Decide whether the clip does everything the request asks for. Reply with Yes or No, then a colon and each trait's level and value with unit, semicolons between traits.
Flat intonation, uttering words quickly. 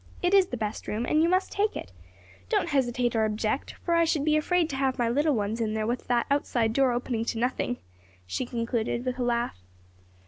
No: average, 4.3 semitones; fast, 230 wpm